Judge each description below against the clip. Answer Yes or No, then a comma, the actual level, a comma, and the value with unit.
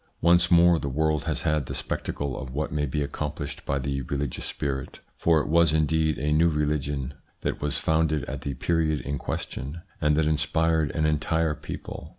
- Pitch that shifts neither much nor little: No, narrow, 2.0 semitones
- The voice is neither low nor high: No, very low, 75 Hz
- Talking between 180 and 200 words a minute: Yes, average, 185 wpm